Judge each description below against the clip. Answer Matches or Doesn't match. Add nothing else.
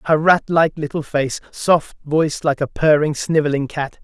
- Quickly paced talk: Doesn't match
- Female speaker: Doesn't match